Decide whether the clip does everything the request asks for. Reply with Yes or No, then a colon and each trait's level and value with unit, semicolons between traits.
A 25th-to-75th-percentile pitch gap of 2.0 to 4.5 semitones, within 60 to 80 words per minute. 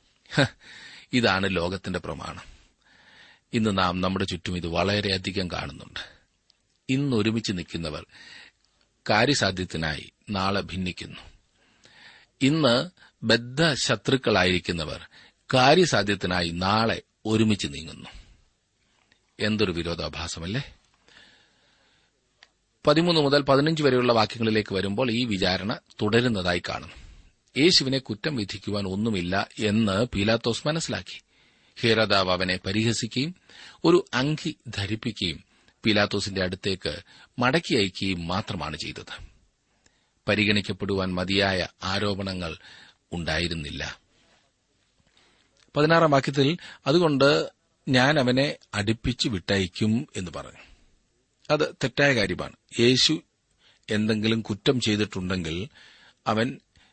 No: average, 5.0 semitones; average, 75 wpm